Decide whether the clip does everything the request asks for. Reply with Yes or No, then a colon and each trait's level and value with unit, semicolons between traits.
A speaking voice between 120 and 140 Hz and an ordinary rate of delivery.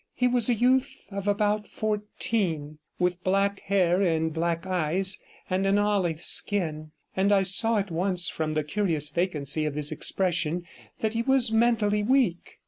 No: high, 190 Hz; average, 160 wpm